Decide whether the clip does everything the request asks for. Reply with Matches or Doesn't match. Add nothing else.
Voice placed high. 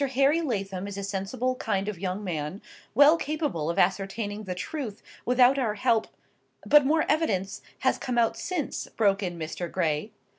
Matches